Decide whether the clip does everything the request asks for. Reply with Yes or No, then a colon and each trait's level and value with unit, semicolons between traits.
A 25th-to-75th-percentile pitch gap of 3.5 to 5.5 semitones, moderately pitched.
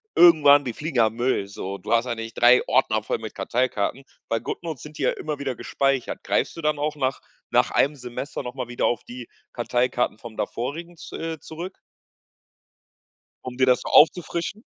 No: average, 4.0 semitones; low, 130 Hz